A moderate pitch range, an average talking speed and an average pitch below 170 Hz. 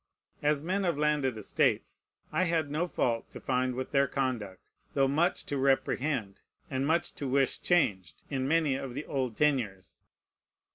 Yes: average, 3.0 semitones; average, 160 wpm; low, 135 Hz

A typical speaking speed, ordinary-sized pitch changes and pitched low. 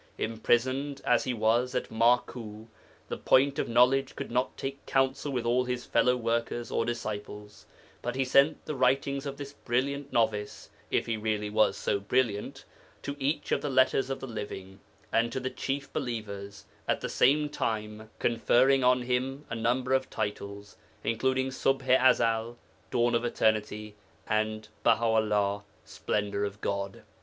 Yes: average, 160 wpm; average, 3.4 semitones; low, 120 Hz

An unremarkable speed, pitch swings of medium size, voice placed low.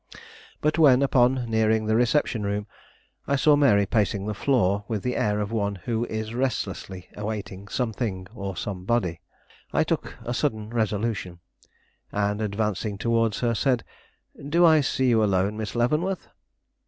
Yes: average, 150 wpm; average, 3.3 semitones; low, 110 Hz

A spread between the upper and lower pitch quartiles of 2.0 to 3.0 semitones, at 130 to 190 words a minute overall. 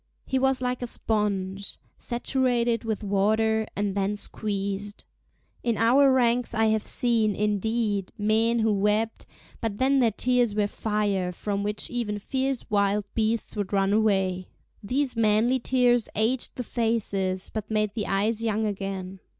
Yes: average, 2.7 semitones; average, 150 wpm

